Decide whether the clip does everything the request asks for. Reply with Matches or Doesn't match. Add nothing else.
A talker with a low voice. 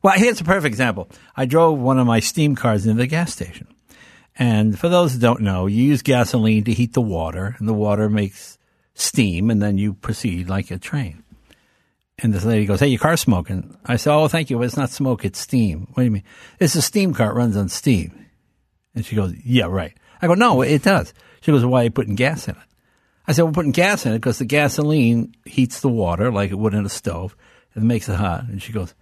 Matches